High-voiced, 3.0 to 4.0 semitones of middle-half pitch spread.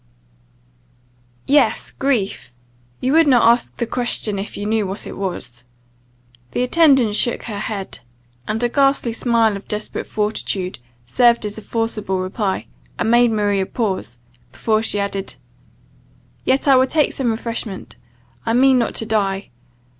Yes: high, 220 Hz; average, 3.4 semitones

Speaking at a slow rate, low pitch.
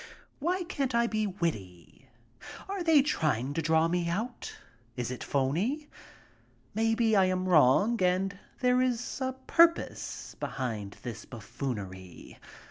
No: slow, 130 wpm; medium, 185 Hz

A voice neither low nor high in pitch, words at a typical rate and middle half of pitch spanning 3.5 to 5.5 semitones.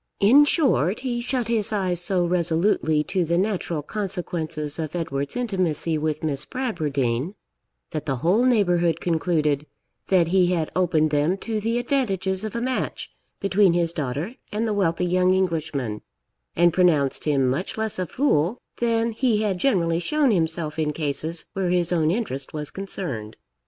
Yes: medium, 175 Hz; average, 160 wpm; average, 5.1 semitones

